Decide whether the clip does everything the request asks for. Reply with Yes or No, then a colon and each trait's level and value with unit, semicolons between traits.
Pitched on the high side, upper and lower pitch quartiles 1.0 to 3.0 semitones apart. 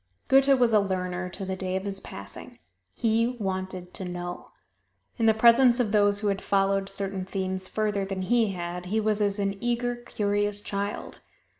Yes: high, 200 Hz; narrow, 2.6 semitones